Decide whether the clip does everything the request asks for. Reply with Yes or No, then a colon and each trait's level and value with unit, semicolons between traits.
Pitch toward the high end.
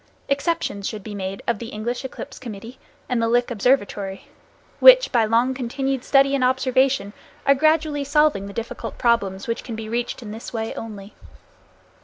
Yes: high, 240 Hz